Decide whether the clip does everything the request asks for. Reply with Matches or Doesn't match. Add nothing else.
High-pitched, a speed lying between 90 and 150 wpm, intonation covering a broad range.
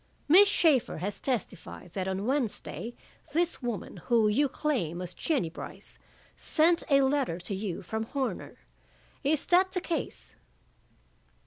Matches